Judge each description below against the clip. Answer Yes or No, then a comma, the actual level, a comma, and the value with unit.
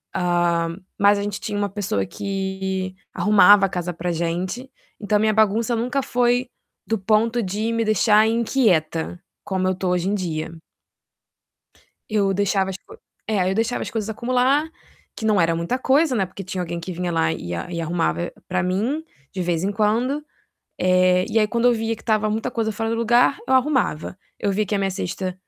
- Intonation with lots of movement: No, average, 3.7 semitones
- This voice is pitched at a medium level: No, high, 200 Hz